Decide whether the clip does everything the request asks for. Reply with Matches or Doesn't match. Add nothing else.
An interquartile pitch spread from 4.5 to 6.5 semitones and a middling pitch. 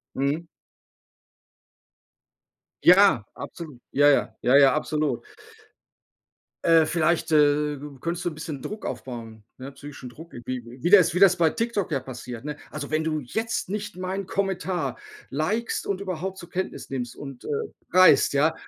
Matches